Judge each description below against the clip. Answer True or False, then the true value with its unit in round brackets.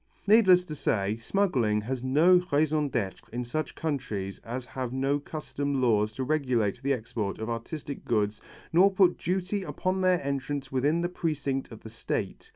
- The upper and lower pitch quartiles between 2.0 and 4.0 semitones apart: False (5.6 semitones)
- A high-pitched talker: False (135 Hz)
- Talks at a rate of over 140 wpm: True (165 wpm)